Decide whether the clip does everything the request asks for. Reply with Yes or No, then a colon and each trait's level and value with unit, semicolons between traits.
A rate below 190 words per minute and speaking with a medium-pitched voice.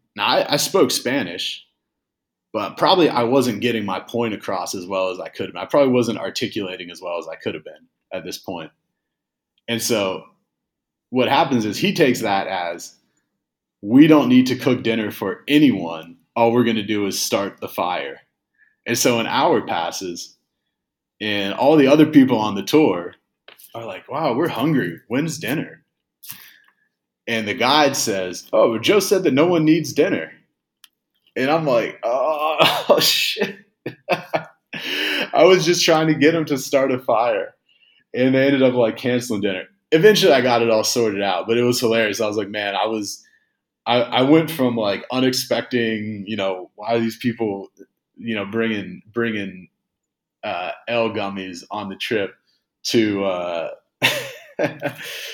No: average, 170 wpm; low, 115 Hz